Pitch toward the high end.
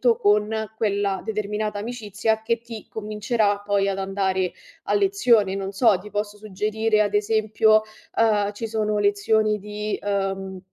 Yes: high, 210 Hz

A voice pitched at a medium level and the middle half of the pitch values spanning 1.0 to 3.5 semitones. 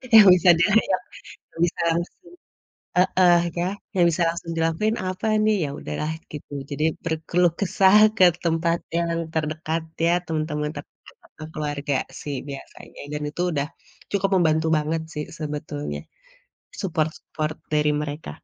Yes: medium, 165 Hz; average, 3.0 semitones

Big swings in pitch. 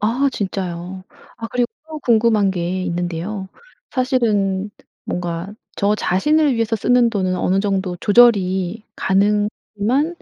No: average, 3.9 semitones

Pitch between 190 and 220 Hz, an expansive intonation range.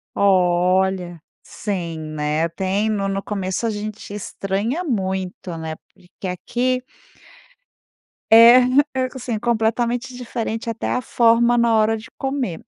No: high, 215 Hz; average, 4.2 semitones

